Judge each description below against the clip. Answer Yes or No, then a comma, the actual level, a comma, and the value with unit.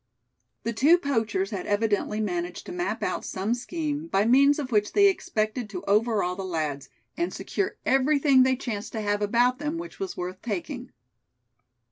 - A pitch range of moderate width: No, wide, 5.9 semitones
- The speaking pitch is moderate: No, high, 230 Hz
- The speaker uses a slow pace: No, average, 170 wpm